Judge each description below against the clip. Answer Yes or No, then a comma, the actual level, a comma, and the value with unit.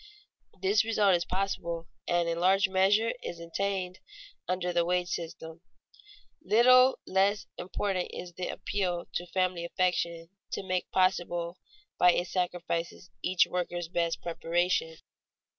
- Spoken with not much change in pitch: Yes, narrow, 1.8 semitones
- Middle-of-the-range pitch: Yes, medium, 180 Hz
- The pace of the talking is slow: Yes, slow, 125 wpm